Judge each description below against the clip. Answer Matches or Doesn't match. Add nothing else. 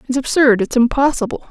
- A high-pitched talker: Matches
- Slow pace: Matches